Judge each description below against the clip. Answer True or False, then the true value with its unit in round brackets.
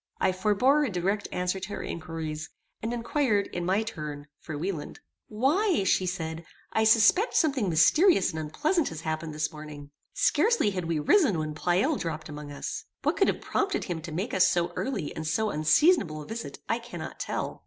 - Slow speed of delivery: False (185 wpm)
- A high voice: False (180 Hz)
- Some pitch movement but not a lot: False (6.7 semitones)